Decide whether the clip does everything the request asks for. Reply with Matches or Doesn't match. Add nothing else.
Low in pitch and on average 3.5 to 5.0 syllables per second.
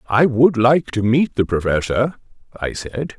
Matches